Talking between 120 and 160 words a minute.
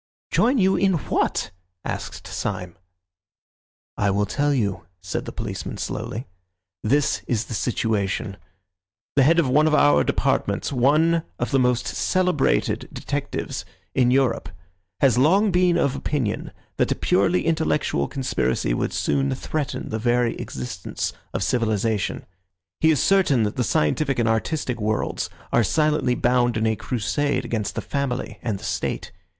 Yes: average, 145 wpm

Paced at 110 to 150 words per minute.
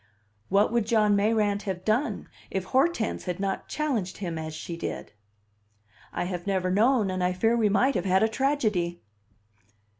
No: average, 170 wpm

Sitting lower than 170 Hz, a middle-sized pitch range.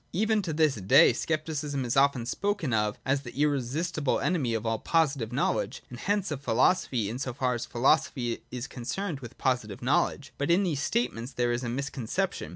Yes: low, 135 Hz; average, 4.5 semitones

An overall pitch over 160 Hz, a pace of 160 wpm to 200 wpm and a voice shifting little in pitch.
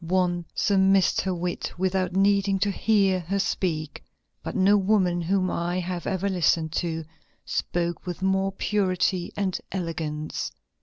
No: medium, 185 Hz; average, 140 wpm; narrow, 1.9 semitones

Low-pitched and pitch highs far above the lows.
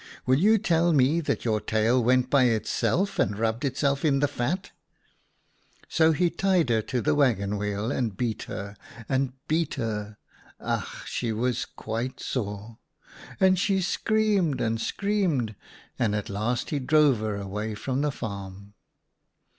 Yes: low, 125 Hz; wide, 6.2 semitones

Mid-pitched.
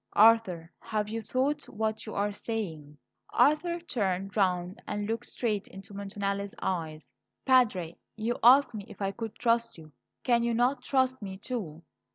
No: high, 215 Hz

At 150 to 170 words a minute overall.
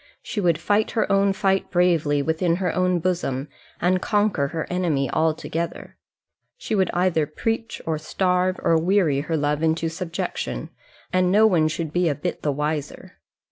Yes: average, 165 wpm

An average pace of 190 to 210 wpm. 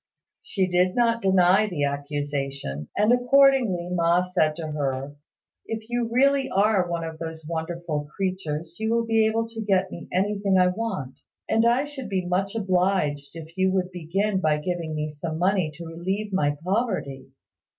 No: average, 170 wpm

